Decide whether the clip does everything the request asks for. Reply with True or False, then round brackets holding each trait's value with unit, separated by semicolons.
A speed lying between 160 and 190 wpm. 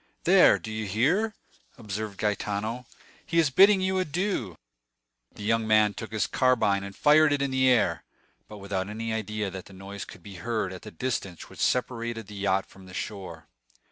True (185 wpm)